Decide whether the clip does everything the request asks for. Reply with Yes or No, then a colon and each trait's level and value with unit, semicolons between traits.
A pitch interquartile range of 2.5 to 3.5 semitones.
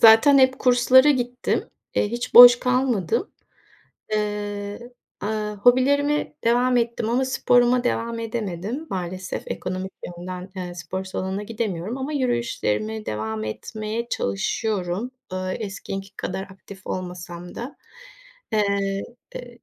No: average, 4.5 semitones